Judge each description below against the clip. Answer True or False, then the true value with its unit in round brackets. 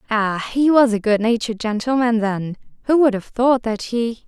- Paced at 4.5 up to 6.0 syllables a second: True (4.9 syllables/s)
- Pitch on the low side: False (230 Hz)